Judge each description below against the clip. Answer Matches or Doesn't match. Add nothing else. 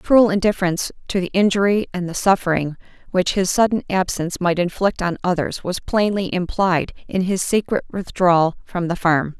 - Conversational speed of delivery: Matches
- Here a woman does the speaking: Matches